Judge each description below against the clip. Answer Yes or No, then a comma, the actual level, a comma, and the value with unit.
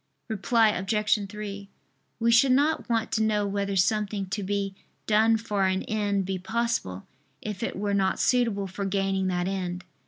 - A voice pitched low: No, high, 200 Hz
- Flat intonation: Yes, narrow, 2.2 semitones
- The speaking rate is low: No, average, 165 wpm